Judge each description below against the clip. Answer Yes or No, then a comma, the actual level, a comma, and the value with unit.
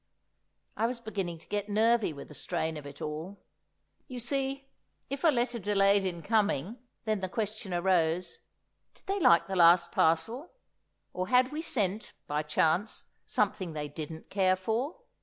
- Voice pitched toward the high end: Yes, high, 195 Hz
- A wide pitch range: Yes, wide, 5.8 semitones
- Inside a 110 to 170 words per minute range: Yes, average, 160 wpm